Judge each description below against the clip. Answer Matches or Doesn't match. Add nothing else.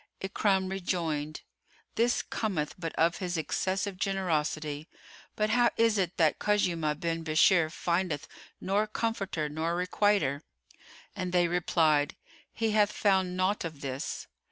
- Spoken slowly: Matches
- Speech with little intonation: Doesn't match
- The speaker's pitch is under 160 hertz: Doesn't match